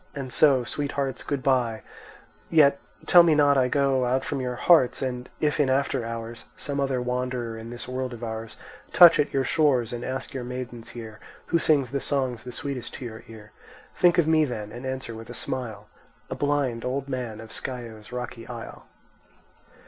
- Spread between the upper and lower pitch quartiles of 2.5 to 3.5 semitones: Yes, average, 2.9 semitones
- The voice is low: Yes, low, 125 Hz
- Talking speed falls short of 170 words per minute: No, average, 185 wpm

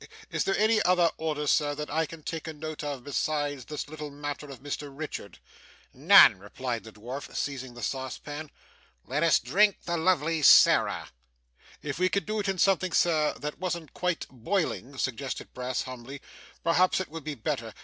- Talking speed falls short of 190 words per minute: Yes, average, 180 wpm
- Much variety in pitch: No, average, 3.6 semitones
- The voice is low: No, medium, 150 Hz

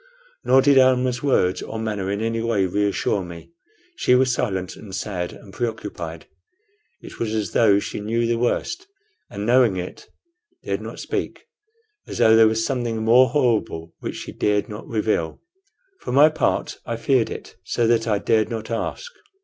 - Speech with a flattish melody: No, average, 3.1 semitones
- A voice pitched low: Yes, low, 110 Hz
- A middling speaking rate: Yes, average, 175 wpm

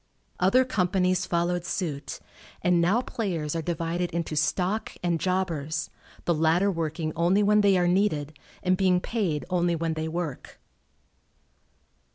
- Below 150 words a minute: Yes, average, 140 wpm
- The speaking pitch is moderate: Yes, medium, 175 Hz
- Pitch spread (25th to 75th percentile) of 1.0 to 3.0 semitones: Yes, narrow, 2.5 semitones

